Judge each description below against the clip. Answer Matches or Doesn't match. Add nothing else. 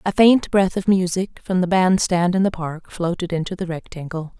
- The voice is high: Doesn't match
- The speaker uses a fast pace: Matches